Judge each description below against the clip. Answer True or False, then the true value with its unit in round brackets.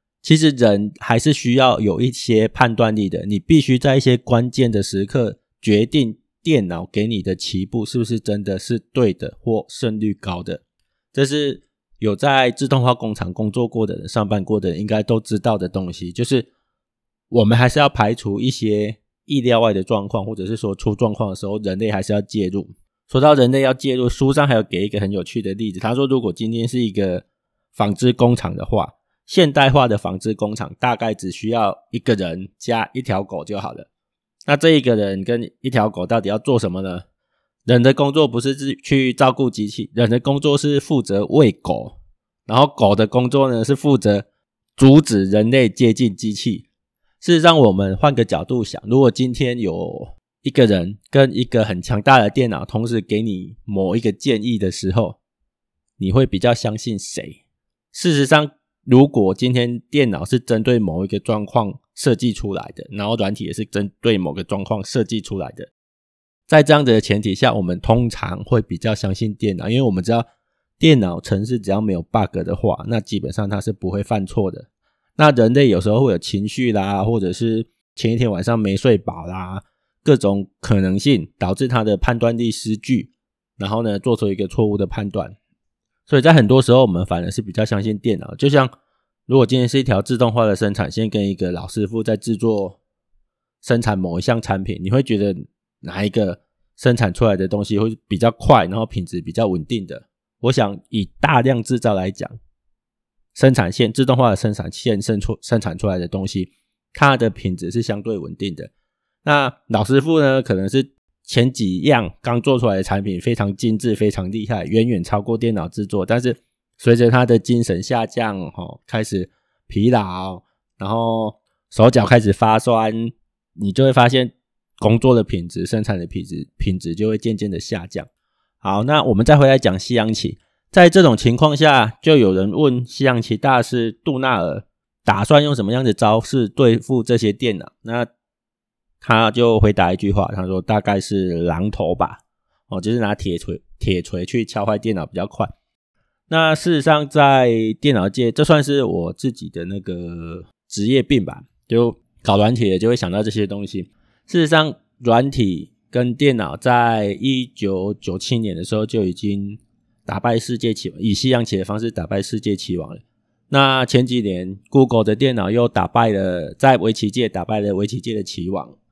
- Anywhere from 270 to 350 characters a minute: True (275 characters per minute)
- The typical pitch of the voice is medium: False (110 Hz)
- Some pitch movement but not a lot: True (3.7 semitones)